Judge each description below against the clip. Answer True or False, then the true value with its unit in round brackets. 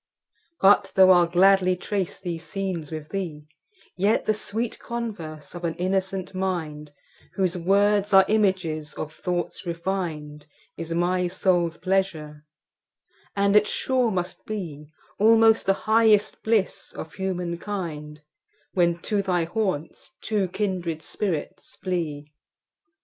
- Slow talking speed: True (110 wpm)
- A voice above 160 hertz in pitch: True (185 Hz)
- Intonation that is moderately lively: True (3.3 semitones)